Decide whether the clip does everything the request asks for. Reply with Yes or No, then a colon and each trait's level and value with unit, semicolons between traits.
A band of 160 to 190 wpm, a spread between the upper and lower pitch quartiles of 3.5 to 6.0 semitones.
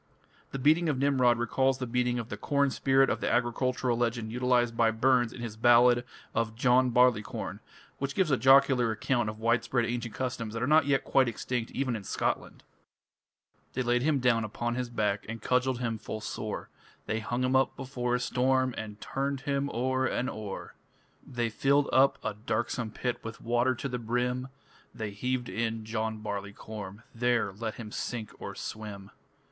No: average, 180 wpm; narrow, 2.4 semitones